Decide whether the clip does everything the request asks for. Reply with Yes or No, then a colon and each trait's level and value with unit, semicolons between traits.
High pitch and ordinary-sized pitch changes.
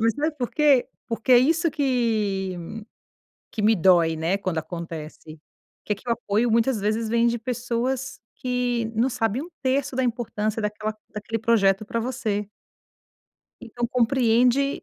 Yes: high, 230 Hz; average, 3.3 semitones